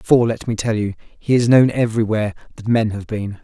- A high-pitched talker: No, low, 110 Hz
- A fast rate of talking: Yes, fast, 225 wpm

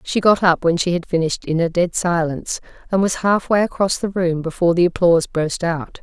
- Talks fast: Yes, fast, 220 wpm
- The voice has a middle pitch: Yes, medium, 175 Hz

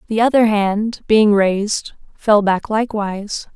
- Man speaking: No, female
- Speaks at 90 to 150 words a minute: Yes, slow, 135 wpm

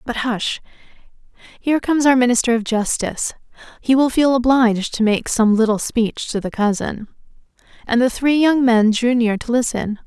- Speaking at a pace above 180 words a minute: No, average, 175 wpm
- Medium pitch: No, high, 235 Hz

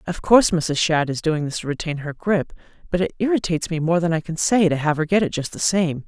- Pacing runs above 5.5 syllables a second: Yes, 6.0 syllables/s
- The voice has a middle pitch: Yes, medium, 165 Hz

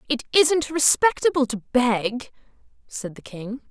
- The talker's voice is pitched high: Yes, very high, 260 Hz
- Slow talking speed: Yes, slow, 130 wpm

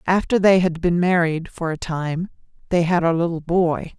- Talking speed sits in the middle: Yes, average, 195 wpm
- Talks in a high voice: No, medium, 170 Hz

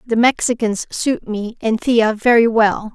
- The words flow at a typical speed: Yes, average, 165 wpm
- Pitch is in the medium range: No, high, 225 Hz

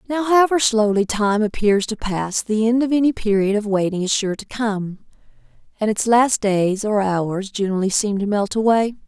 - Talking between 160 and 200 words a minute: Yes, average, 190 wpm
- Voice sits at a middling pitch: No, high, 215 Hz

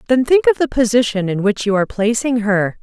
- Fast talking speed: Yes, fast, 235 wpm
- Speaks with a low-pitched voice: No, high, 225 Hz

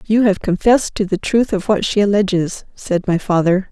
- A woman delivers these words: Yes, female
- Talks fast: Yes, fast, 210 wpm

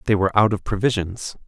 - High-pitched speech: No, low, 100 Hz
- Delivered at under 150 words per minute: No, fast, 205 wpm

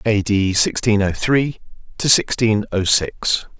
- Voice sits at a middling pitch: No, low, 105 Hz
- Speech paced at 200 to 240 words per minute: No, average, 150 wpm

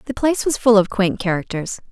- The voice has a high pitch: Yes, high, 215 Hz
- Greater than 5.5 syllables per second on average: Yes, 6.0 syllables/s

